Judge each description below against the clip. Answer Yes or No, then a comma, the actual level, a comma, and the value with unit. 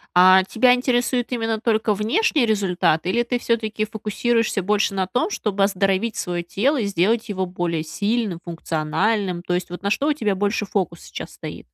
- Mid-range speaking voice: No, high, 205 Hz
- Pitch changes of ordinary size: Yes, average, 3.8 semitones